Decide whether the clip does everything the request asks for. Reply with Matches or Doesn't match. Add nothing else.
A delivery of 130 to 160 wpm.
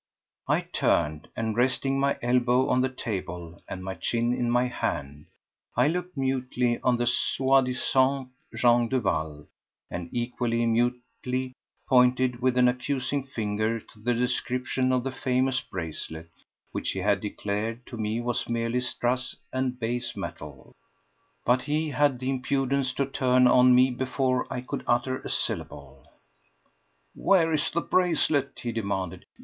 Matches